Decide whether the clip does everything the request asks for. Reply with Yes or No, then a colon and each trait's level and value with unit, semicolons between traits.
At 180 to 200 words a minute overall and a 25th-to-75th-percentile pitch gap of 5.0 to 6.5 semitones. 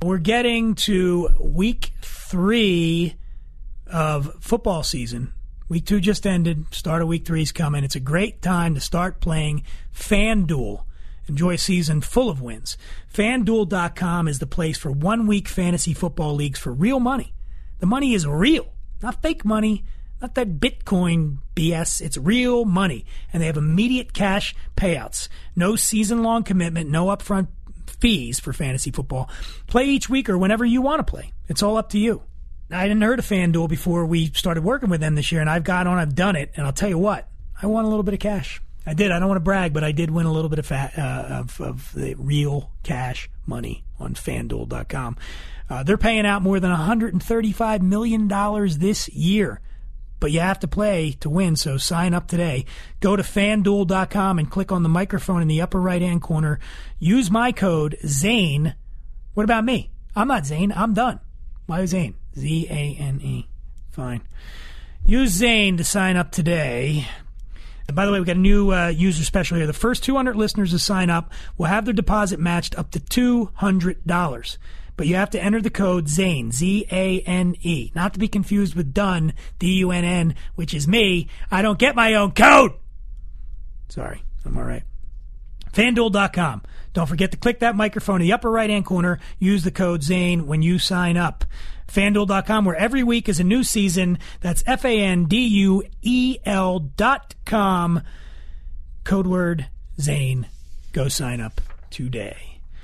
Yes: average, 185 wpm; wide, 5.4 semitones